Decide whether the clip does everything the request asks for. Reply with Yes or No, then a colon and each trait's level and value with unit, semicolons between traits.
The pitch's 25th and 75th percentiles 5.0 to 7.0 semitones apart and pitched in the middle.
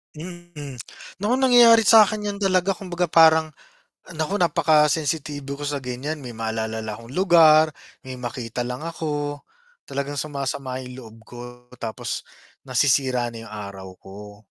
Yes: wide, 5.5 semitones; medium, 145 Hz